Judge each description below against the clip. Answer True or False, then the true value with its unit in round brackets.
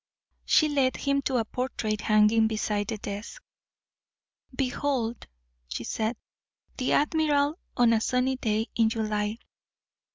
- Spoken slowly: True (125 wpm)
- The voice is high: True (230 Hz)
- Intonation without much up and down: False (3.7 semitones)